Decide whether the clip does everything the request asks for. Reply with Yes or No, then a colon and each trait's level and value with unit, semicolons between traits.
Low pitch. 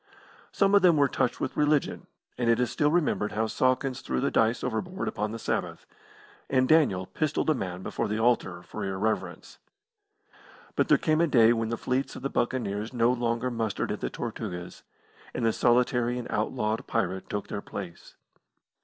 Yes: low, 120 Hz